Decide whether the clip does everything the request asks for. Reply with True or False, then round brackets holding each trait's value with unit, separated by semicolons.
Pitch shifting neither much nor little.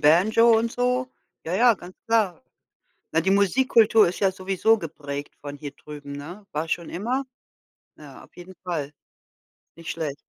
False (6.3 semitones)